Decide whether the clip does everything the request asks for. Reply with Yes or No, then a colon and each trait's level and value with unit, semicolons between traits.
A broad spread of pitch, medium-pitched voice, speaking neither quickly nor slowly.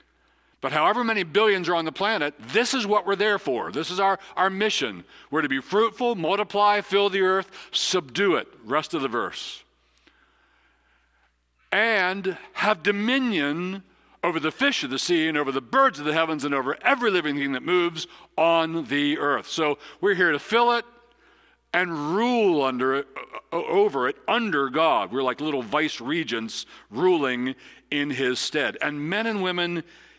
Yes: wide, 5.9 semitones; medium, 175 Hz; average, 170 wpm